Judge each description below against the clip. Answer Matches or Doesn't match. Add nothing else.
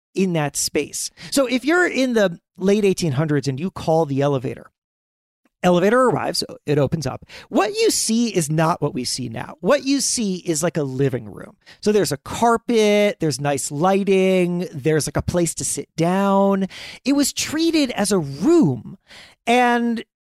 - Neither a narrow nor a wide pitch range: Doesn't match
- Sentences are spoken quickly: Doesn't match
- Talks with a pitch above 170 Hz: Matches